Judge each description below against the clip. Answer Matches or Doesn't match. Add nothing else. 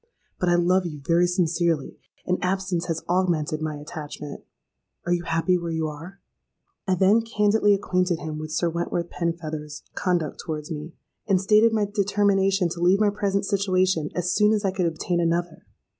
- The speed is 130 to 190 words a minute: Matches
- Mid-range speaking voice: Matches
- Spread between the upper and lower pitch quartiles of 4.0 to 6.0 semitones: Doesn't match